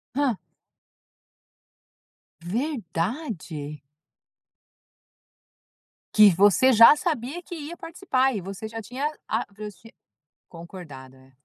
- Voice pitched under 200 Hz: No, high, 215 Hz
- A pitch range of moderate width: No, wide, 7.7 semitones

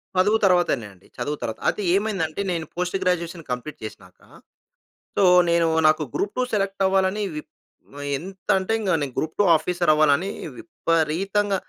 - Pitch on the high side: No, medium, 180 Hz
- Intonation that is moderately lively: Yes, average, 3.9 semitones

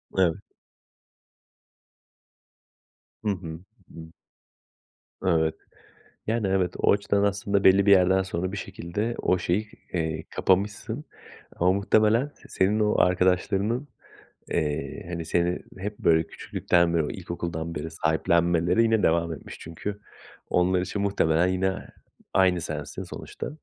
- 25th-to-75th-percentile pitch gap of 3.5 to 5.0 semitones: No, average, 3.1 semitones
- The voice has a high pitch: No, very low, 90 Hz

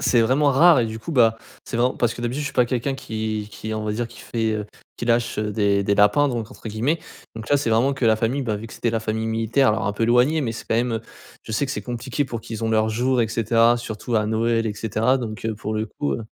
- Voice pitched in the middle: No, low, 115 Hz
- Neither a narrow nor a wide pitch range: No, narrow, 2.1 semitones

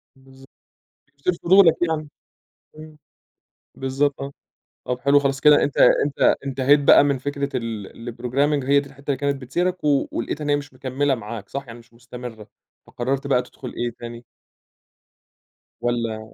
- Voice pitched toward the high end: No, low, 135 Hz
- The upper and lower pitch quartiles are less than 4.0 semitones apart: Yes, average, 2.9 semitones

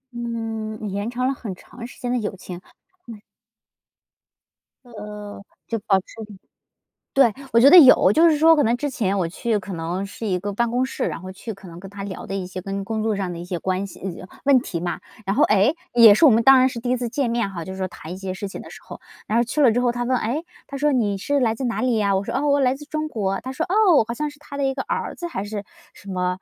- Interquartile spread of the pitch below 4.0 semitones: No, average, 4.8 semitones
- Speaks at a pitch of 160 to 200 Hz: No, high, 225 Hz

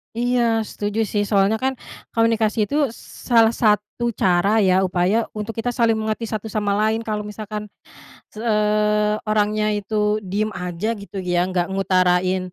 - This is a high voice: Yes, high, 210 Hz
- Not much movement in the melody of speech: Yes, narrow, 2.2 semitones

